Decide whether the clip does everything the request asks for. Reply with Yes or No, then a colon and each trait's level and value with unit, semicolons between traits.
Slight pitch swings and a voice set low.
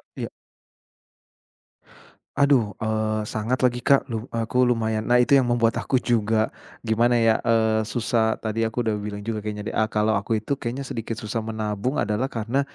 Yes: narrow, 1.9 semitones; low, 115 Hz